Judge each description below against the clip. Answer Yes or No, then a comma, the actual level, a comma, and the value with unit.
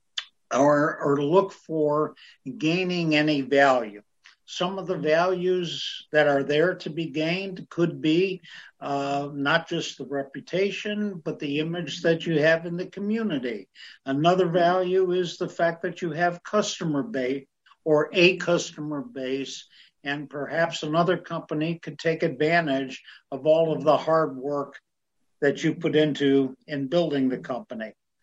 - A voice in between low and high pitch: Yes, medium, 160 Hz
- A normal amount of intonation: Yes, average, 3.6 semitones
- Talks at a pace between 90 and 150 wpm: Yes, average, 145 wpm